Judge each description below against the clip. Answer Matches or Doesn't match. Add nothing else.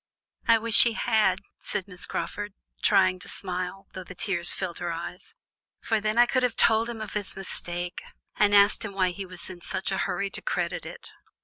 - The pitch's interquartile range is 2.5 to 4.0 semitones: Matches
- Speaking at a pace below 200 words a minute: Doesn't match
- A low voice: Doesn't match